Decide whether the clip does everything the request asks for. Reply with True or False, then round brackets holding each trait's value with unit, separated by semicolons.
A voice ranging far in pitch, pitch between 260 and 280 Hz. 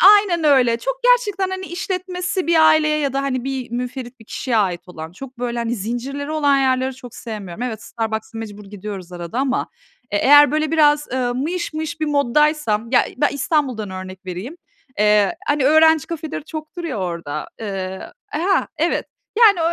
True (6.2 semitones; 270 Hz)